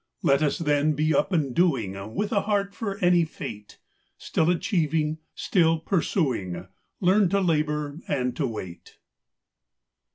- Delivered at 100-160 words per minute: Yes, slow, 135 wpm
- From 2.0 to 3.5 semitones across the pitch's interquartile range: No, average, 4.7 semitones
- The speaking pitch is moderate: Yes, medium, 155 Hz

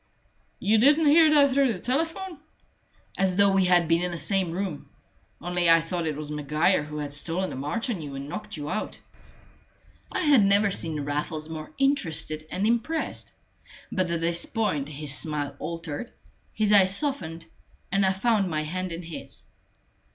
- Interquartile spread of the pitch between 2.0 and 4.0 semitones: No, wide, 5.5 semitones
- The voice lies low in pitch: No, medium, 180 Hz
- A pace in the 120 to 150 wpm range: No, average, 175 wpm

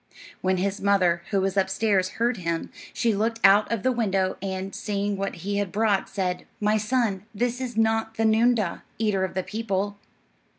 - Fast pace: No, average, 180 wpm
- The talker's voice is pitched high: Yes, high, 200 Hz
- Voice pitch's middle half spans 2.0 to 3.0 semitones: Yes, average, 2.7 semitones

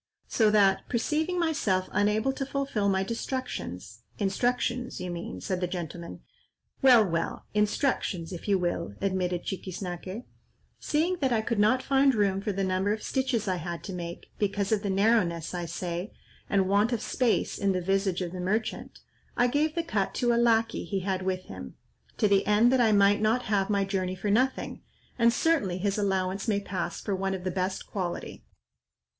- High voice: Yes, high, 200 Hz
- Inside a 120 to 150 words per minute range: No, average, 180 wpm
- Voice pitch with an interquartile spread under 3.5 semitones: No, average, 4.0 semitones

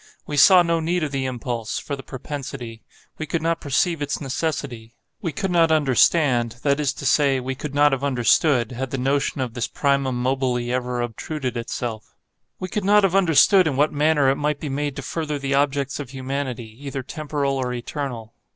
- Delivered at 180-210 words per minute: Yes, average, 190 wpm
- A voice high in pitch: No, medium, 140 Hz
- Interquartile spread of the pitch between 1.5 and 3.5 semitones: Yes, average, 3.1 semitones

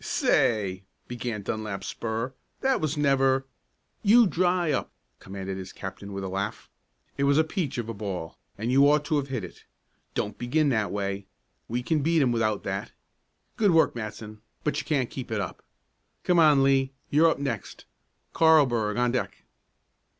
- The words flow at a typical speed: Yes, average, 175 wpm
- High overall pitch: No, low, 125 Hz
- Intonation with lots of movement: Yes, wide, 6.0 semitones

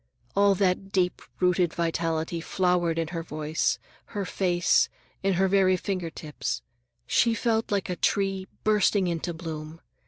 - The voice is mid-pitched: Yes, medium, 180 Hz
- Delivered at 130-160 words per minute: Yes, average, 145 wpm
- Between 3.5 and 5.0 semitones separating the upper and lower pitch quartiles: No, average, 2.8 semitones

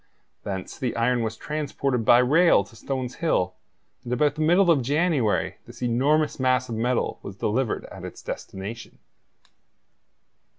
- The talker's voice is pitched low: Yes, low, 125 Hz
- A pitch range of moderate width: Yes, average, 4.5 semitones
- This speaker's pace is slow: No, average, 145 wpm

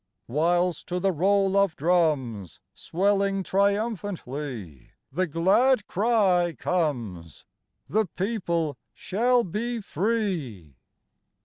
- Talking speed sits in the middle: No, slow, 90 wpm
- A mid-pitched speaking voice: Yes, medium, 180 Hz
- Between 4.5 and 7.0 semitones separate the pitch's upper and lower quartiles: Yes, average, 5.2 semitones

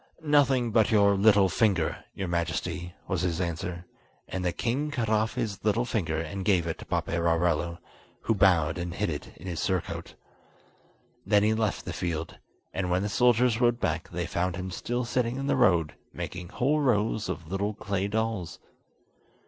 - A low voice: Yes, very low, 95 Hz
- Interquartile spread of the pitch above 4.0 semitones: Yes, average, 4.4 semitones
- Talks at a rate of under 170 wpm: No, average, 175 wpm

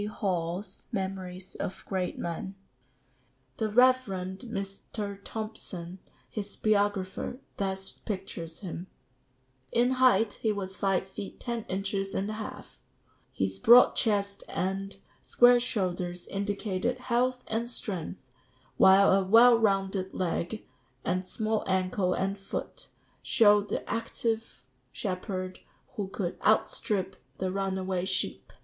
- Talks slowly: Yes, slow, 115 wpm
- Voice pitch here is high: Yes, high, 195 Hz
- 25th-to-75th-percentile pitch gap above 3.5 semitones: No, narrow, 2.6 semitones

